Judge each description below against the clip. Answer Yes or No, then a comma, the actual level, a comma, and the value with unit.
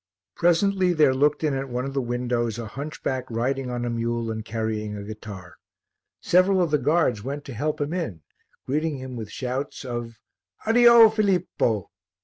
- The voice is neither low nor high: No, low, 130 Hz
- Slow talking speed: No, average, 170 wpm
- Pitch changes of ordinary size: Yes, average, 5.0 semitones